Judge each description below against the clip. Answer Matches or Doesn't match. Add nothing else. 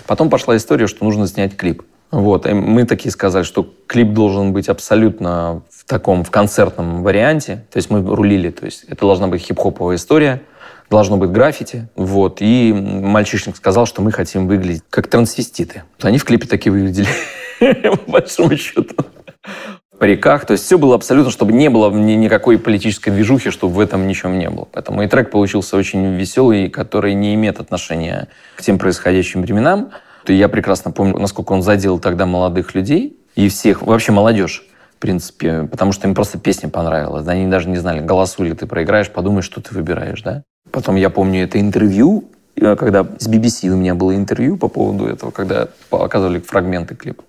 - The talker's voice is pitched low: Matches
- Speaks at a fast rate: Matches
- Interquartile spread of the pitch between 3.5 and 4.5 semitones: Doesn't match